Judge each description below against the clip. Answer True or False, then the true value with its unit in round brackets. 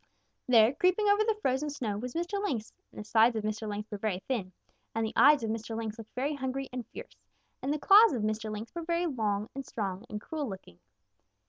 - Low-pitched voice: False (235 Hz)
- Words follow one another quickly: True (225 wpm)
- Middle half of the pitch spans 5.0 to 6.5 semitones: True (5.4 semitones)